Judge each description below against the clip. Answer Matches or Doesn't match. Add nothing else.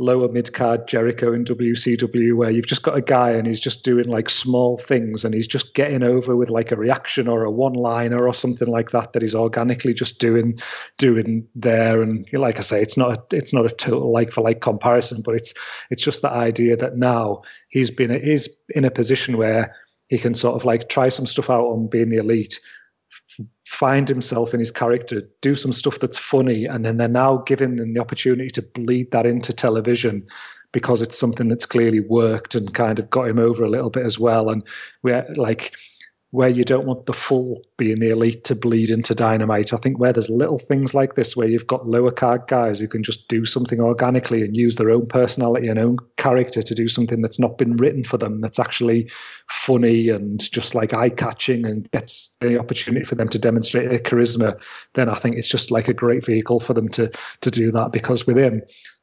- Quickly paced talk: Matches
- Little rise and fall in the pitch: Matches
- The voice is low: Matches